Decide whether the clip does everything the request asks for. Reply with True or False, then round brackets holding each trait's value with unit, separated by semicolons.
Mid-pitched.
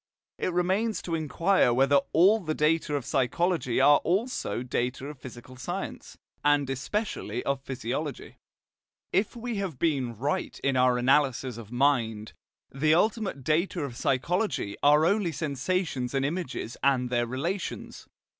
True (145 Hz)